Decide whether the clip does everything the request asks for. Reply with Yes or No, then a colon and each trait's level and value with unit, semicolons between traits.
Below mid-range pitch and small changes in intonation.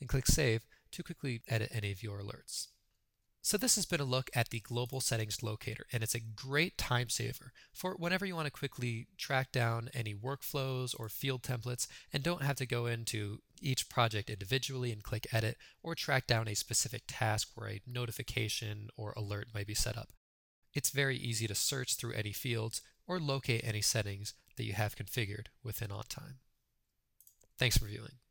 No: low, 120 Hz; average, 3.3 semitones